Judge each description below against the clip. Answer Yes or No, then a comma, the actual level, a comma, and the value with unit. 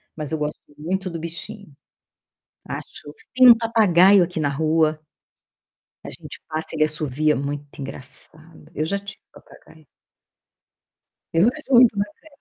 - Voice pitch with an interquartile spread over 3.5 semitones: Yes, average, 4.7 semitones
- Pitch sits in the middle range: Yes, medium, 160 Hz